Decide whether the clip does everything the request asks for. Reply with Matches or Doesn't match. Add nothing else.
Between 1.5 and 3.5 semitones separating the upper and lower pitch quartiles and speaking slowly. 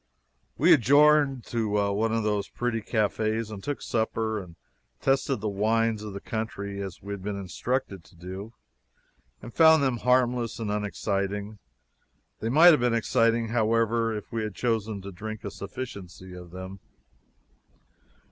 Doesn't match